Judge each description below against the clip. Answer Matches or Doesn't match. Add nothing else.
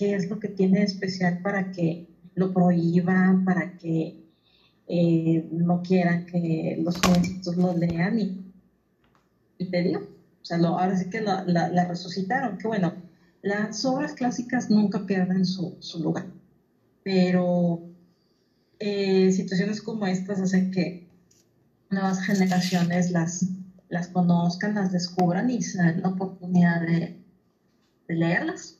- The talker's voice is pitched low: Doesn't match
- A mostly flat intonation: Matches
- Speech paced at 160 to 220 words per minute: Doesn't match